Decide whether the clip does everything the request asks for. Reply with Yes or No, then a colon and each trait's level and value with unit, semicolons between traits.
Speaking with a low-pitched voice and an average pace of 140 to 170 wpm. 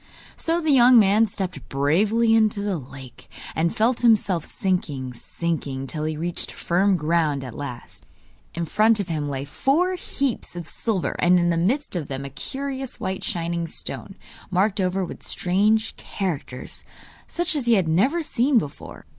No: medium, 185 Hz; average, 165 wpm